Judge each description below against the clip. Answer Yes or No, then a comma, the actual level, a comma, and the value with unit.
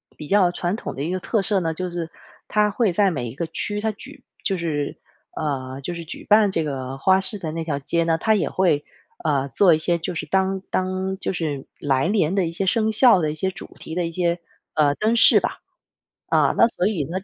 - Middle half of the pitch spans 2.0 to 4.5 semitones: Yes, average, 3.8 semitones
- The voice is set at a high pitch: No, medium, 175 Hz